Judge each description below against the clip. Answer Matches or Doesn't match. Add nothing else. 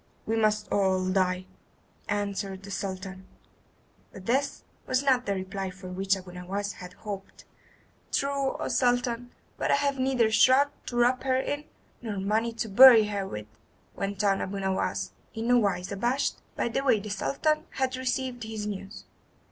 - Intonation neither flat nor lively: Matches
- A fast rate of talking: Doesn't match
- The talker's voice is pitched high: Matches